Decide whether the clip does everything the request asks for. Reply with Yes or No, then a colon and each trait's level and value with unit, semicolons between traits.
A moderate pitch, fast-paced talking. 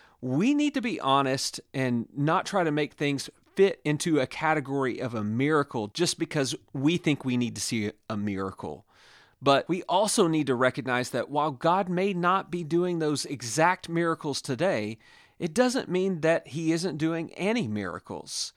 No: medium, 150 Hz; average, 175 wpm